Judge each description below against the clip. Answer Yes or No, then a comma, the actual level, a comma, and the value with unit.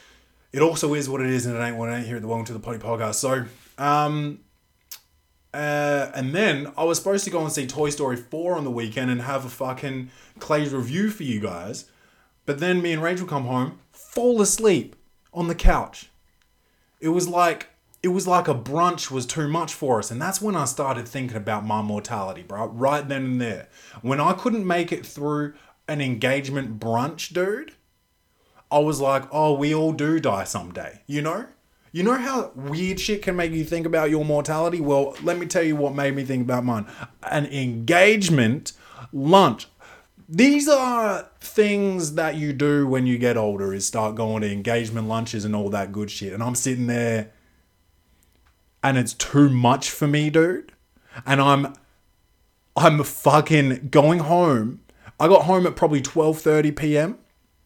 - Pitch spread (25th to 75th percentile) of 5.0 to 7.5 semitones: Yes, wide, 5.6 semitones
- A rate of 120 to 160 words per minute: No, average, 185 wpm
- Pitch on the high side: No, medium, 140 Hz